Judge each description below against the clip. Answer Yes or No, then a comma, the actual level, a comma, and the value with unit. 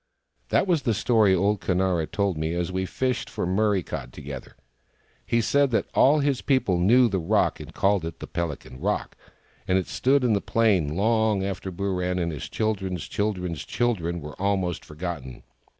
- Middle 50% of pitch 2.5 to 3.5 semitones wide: No, average, 4.2 semitones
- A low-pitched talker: Yes, very low, 95 Hz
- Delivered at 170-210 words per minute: Yes, average, 180 wpm